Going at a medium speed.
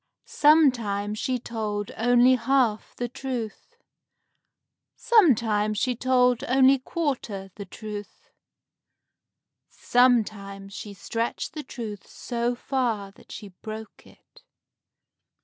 No: slow, 95 wpm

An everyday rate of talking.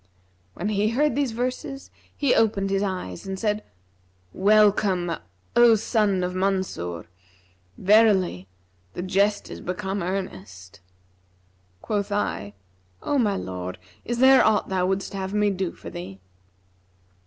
No: slow, 130 wpm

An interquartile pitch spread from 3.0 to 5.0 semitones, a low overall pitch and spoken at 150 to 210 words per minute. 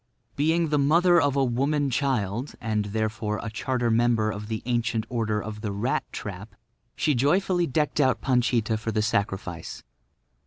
Yes: average, 4.6 semitones; low, 120 Hz; average, 160 wpm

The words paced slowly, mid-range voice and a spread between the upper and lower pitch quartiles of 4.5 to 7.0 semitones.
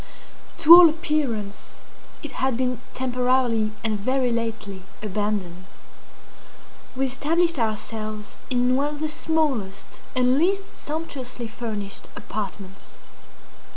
No: slow, 105 wpm; very high, 250 Hz; average, 5.3 semitones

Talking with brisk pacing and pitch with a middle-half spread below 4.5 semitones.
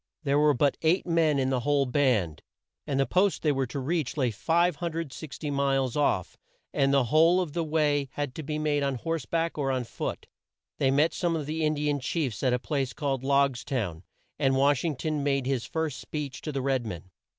Yes: fast, 215 wpm; average, 2.8 semitones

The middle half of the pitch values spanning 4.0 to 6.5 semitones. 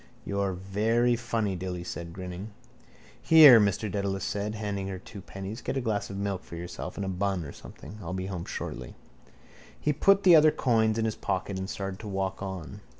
No: average, 2.9 semitones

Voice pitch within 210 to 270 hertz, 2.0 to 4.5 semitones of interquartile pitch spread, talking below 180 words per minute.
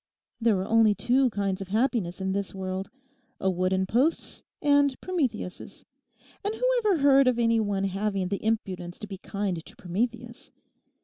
No: high, 215 Hz; average, 5.1 semitones; average, 160 wpm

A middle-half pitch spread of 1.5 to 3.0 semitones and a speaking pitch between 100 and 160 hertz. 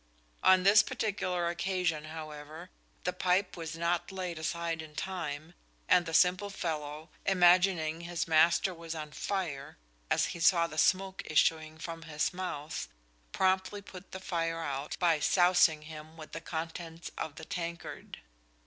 No: narrow, 2.5 semitones; medium, 170 Hz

